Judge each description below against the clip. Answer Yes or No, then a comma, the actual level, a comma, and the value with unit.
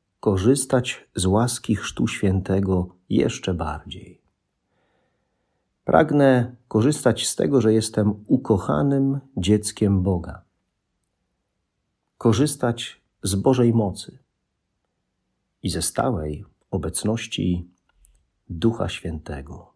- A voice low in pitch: Yes, low, 100 Hz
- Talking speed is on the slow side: Yes, slow, 80 wpm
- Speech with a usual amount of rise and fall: Yes, average, 4.8 semitones